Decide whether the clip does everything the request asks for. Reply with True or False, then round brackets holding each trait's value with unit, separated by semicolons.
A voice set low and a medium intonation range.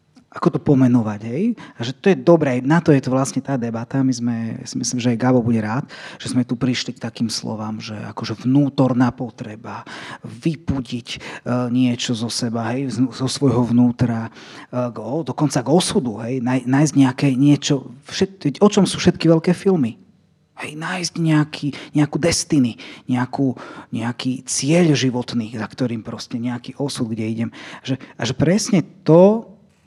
True (130 Hz; 4.1 semitones)